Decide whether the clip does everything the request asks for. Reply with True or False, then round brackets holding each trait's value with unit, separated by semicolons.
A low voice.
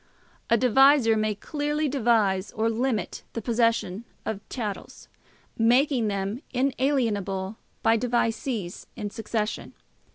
False (230 Hz)